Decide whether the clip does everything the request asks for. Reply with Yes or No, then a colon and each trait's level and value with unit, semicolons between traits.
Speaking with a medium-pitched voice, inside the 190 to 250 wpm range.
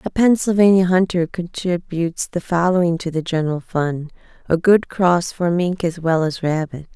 No: medium, 175 Hz; average, 165 wpm